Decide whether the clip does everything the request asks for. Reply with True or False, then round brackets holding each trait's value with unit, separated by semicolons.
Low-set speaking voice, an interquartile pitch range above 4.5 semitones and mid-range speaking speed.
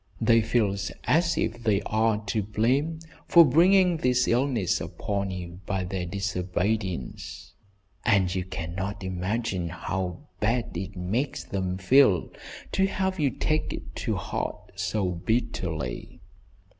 False (105 Hz; 5.2 semitones; 130 wpm)